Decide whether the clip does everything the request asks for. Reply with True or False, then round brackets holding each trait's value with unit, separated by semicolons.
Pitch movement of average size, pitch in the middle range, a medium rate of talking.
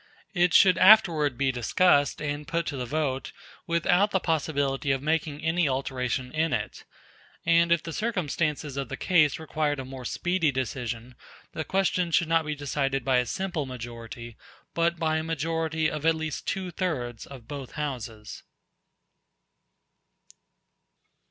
True (3.9 semitones; 150 Hz; 150 wpm)